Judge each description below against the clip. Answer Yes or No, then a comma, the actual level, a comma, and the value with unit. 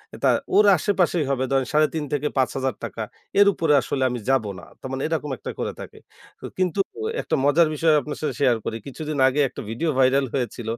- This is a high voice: No, medium, 140 Hz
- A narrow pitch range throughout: No, average, 3.4 semitones